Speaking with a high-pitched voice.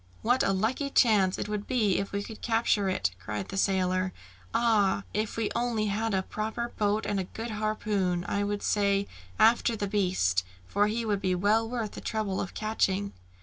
Yes: high, 205 Hz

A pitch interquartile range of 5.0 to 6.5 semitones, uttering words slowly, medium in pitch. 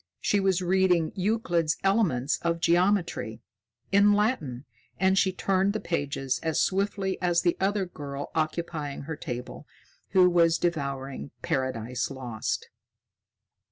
Yes: wide, 5.5 semitones; slow, 120 wpm; medium, 170 Hz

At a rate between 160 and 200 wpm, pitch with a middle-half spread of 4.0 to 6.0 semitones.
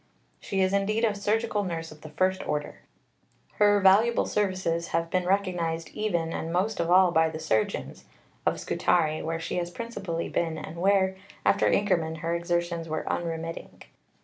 No: average, 165 wpm; average, 3.2 semitones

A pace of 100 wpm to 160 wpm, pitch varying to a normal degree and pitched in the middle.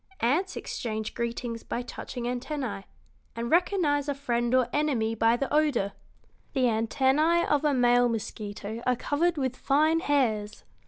No: average, 150 wpm; average, 4.0 semitones; very high, 250 Hz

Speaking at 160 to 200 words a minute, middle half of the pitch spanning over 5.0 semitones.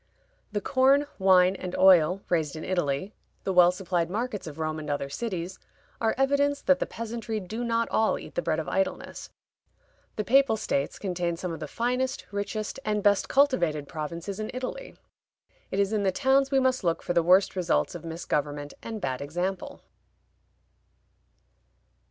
Yes: average, 170 wpm; wide, 5.6 semitones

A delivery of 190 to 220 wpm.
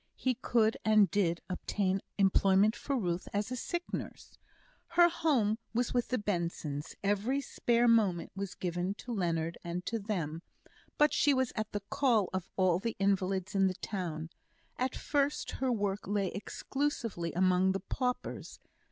No: average, 160 wpm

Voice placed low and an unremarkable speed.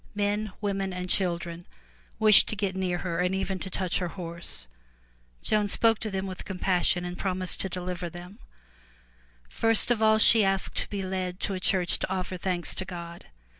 No: medium, 185 Hz; average, 185 wpm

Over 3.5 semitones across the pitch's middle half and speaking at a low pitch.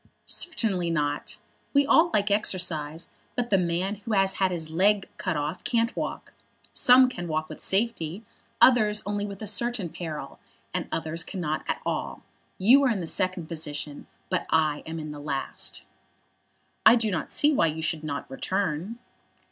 No: average, 5.1 semitones; medium, 185 Hz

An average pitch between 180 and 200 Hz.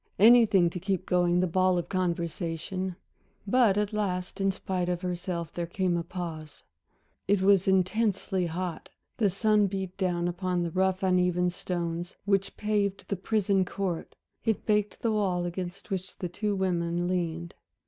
Yes: medium, 185 Hz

